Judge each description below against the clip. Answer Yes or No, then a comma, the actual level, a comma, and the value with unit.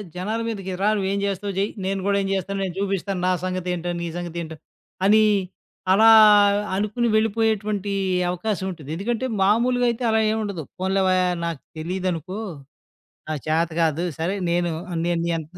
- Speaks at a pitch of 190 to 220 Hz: Yes, high, 195 Hz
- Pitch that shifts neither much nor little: Yes, average, 3.0 semitones